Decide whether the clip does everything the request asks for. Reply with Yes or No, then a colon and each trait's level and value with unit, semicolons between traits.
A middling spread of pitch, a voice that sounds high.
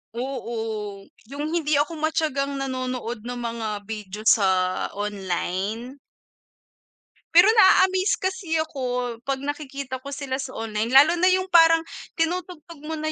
No: wide, 6.1 semitones; very high, 275 Hz